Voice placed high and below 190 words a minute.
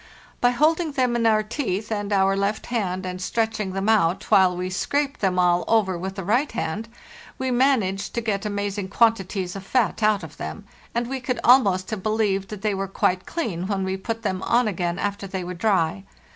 No: high, 205 Hz; fast, 205 wpm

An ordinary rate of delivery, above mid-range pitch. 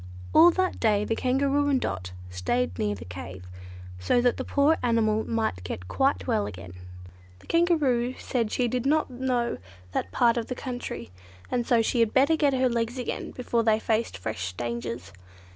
Yes: average, 180 wpm; high, 235 Hz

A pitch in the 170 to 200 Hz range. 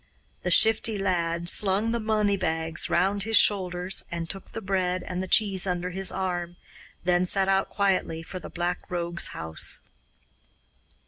Yes: medium, 185 Hz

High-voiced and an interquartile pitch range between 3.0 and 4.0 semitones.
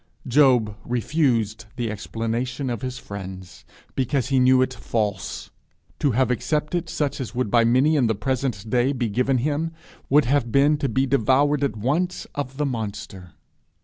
No: low, 125 Hz; average, 3.7 semitones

